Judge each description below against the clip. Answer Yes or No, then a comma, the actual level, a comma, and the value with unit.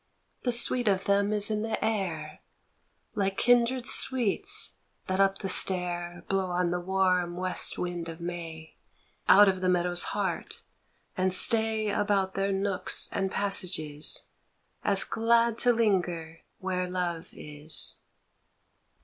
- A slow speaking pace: Yes, slow, 130 wpm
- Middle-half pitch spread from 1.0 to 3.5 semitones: Yes, average, 2.9 semitones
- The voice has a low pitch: No, high, 190 Hz